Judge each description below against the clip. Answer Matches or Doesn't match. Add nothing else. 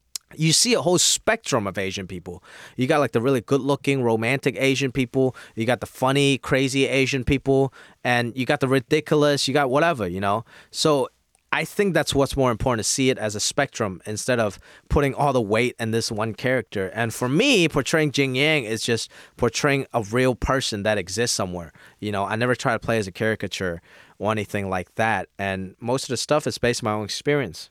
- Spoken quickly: Matches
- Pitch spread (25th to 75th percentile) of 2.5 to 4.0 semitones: Doesn't match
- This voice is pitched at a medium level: Doesn't match